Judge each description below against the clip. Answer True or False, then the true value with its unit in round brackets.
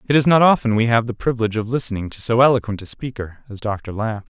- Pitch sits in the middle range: False (115 Hz)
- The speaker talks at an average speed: False (250 wpm)